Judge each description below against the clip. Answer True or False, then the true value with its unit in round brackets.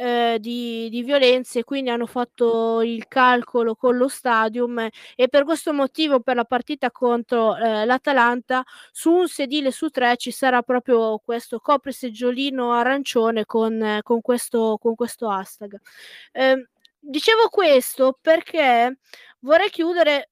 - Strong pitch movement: False (2.8 semitones)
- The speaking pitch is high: True (245 Hz)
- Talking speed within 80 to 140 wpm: True (135 wpm)